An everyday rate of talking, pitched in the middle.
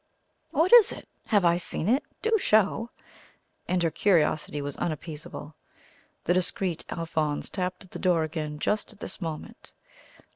Yes: average, 150 wpm; medium, 175 Hz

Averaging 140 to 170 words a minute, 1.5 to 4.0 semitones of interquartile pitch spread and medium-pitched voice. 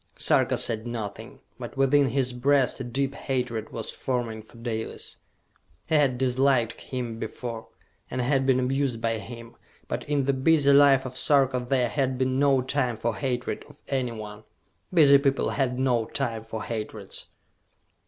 No: average, 160 wpm; average, 2.8 semitones; low, 130 Hz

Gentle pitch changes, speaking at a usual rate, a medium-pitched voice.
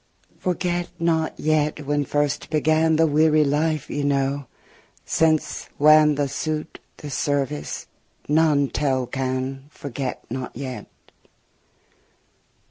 No: narrow, 2.3 semitones; slow, 110 wpm; medium, 145 Hz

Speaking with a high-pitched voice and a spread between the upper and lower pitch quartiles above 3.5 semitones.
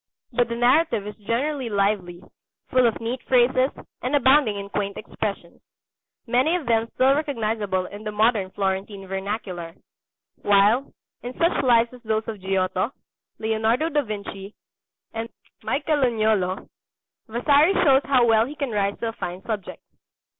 Yes: high, 225 Hz; average, 4.2 semitones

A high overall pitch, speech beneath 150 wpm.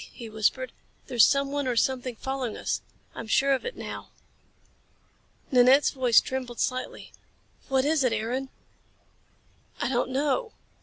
Yes: very high, 260 Hz; slow, 135 wpm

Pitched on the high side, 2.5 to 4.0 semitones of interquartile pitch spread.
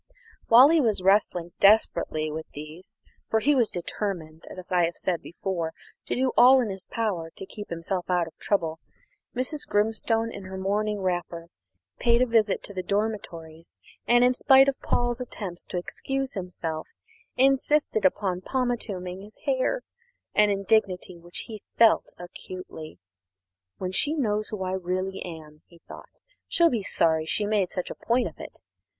No: high, 195 Hz; average, 4.7 semitones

